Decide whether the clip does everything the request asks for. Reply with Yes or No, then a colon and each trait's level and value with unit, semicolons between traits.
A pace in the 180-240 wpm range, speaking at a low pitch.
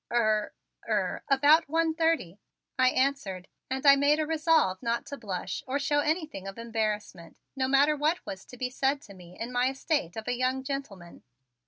No: average, 185 wpm; very high, 260 Hz